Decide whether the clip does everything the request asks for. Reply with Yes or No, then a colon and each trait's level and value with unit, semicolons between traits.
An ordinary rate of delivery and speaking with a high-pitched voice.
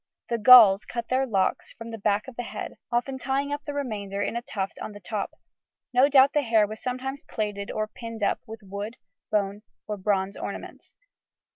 Yes: average, 195 wpm; high, 225 Hz